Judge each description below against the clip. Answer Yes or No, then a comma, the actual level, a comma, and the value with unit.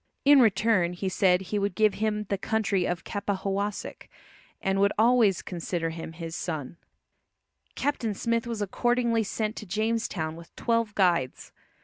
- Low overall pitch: No, high, 200 Hz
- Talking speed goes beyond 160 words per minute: No, average, 145 wpm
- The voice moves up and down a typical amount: Yes, average, 3.9 semitones